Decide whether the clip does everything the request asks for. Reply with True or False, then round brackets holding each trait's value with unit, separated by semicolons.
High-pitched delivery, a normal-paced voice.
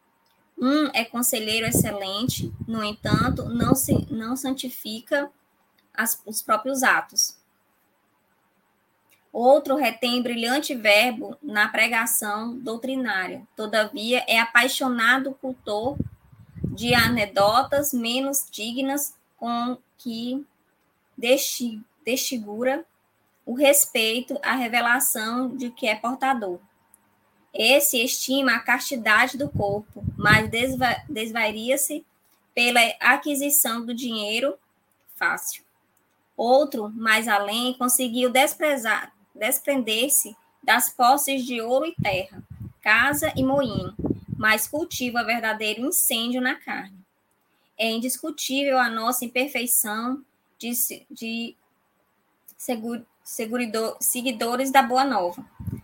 False (250 Hz; 95 wpm)